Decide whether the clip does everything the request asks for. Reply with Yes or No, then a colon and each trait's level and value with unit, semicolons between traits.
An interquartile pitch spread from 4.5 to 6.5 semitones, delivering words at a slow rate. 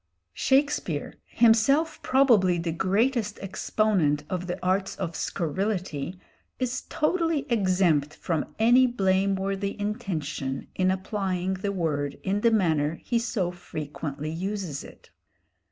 Yes: average, 4.8 semitones; slow, 115 wpm